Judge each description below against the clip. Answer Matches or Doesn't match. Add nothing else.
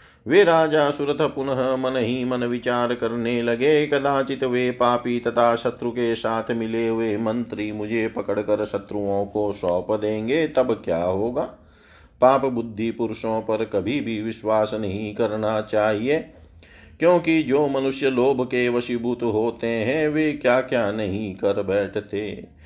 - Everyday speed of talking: Matches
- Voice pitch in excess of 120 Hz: Doesn't match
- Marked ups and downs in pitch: Doesn't match